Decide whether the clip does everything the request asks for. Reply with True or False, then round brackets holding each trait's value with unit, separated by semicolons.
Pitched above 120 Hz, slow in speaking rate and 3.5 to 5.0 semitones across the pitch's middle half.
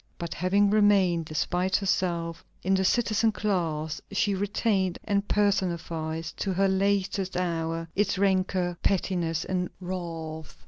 False (185 Hz; 125 wpm; 2.8 semitones)